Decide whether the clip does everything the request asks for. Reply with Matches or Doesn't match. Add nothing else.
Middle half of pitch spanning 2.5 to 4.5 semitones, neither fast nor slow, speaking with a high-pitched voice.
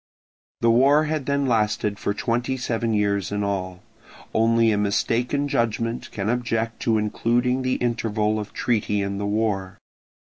Doesn't match